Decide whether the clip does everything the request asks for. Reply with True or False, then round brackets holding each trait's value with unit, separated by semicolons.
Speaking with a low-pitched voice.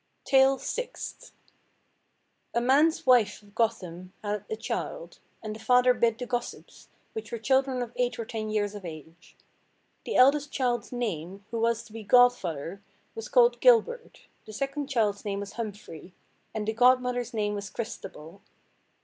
False (230 Hz)